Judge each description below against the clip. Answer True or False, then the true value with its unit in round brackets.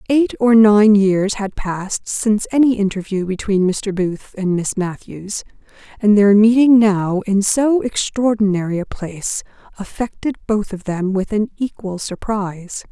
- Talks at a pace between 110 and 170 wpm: True (150 wpm)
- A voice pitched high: True (205 Hz)